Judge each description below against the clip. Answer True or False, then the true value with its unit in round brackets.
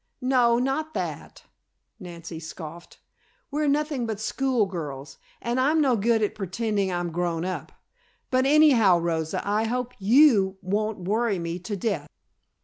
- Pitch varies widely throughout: True (6.2 semitones)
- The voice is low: False (210 Hz)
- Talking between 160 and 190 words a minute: False (140 wpm)